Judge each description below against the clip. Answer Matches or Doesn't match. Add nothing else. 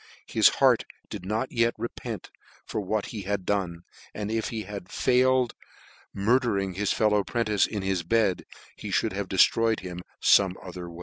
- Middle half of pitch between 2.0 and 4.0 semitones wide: Matches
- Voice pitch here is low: Matches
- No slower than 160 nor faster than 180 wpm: Doesn't match